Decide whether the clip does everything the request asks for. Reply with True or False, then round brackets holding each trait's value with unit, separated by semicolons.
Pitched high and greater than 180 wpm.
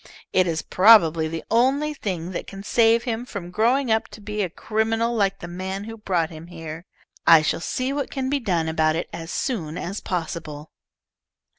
True (195 Hz; 190 wpm)